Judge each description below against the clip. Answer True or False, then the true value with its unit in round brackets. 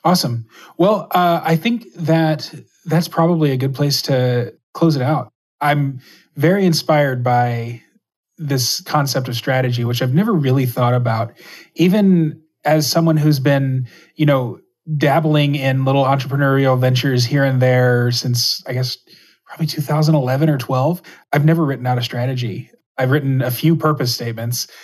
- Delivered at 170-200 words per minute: False (150 wpm)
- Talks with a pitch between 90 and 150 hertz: True (140 Hz)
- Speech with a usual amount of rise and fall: True (3.7 semitones)